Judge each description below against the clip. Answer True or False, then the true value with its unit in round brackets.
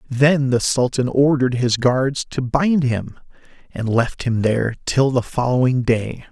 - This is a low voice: True (130 Hz)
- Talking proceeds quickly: False (160 wpm)